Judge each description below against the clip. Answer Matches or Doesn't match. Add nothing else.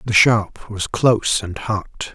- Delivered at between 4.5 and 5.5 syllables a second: Doesn't match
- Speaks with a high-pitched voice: Doesn't match